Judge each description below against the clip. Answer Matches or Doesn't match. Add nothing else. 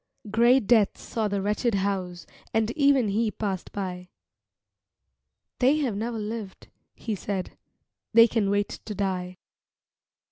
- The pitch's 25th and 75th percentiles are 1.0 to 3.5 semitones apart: Matches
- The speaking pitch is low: Doesn't match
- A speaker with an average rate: Doesn't match